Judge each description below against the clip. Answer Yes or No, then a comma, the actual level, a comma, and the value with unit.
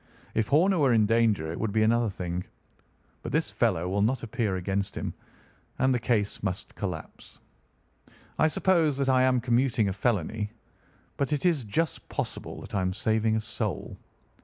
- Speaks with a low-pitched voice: Yes, low, 110 Hz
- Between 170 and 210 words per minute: Yes, average, 175 wpm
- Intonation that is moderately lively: Yes, average, 4.4 semitones